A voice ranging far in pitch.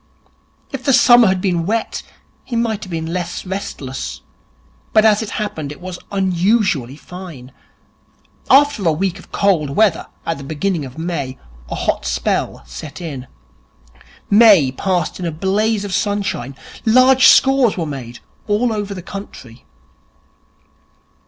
Yes: wide, 5.9 semitones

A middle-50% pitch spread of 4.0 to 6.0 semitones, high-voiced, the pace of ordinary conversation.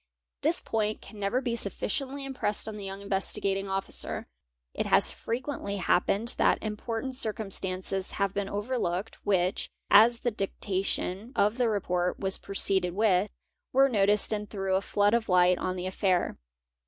No: average, 2.7 semitones; high, 200 Hz; average, 155 wpm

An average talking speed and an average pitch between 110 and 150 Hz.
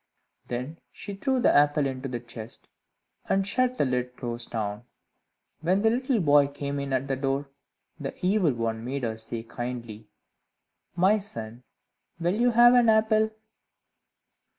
Yes: average, 150 wpm; medium, 140 Hz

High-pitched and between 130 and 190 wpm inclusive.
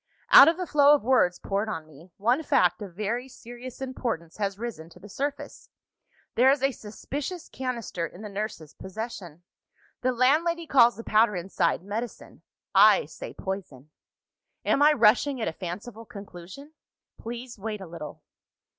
Yes: high, 225 Hz; average, 160 wpm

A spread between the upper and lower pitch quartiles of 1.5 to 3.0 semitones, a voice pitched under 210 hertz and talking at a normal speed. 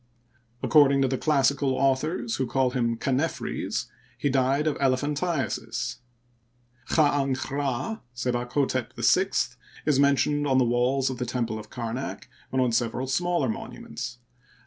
No: narrow, 2.4 semitones; low, 135 Hz; slow, 125 wpm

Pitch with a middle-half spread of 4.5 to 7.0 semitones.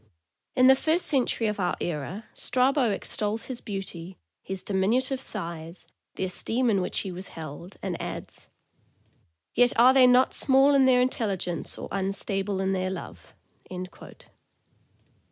Yes: average, 5.2 semitones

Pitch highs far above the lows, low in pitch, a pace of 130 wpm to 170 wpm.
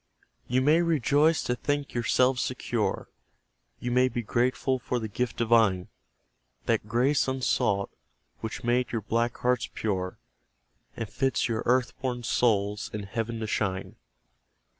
No: average, 2.7 semitones; low, 120 Hz; average, 140 wpm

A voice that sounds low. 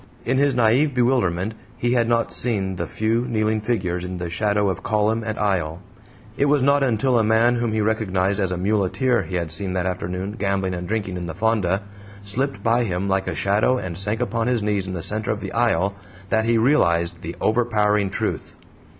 Yes: low, 105 Hz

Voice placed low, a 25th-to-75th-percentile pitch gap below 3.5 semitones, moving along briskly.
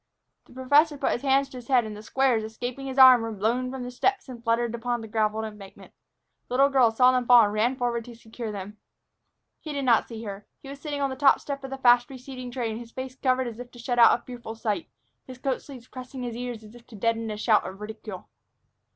No: high, 245 Hz; narrow, 2.6 semitones; fast, 250 wpm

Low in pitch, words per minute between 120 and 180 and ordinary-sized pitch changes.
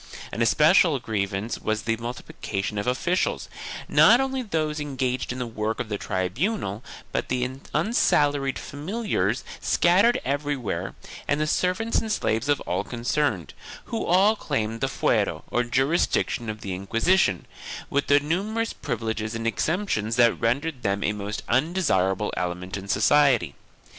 No: low, 125 Hz; average, 145 wpm; wide, 6.9 semitones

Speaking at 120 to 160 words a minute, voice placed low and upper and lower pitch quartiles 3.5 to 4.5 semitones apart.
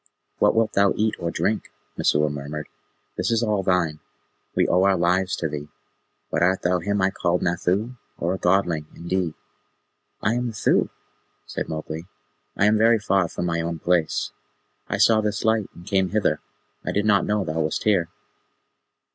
No: average, 175 wpm; very low, 95 Hz; average, 3.8 semitones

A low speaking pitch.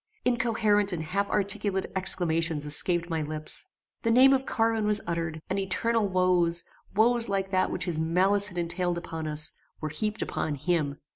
No: medium, 185 Hz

